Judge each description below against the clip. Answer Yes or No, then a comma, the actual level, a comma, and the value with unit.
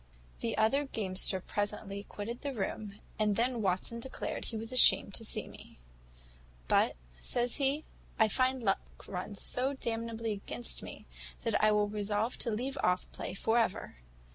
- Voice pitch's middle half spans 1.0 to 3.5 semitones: Yes, average, 3.0 semitones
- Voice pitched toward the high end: Yes, high, 220 Hz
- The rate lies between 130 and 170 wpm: Yes, average, 160 wpm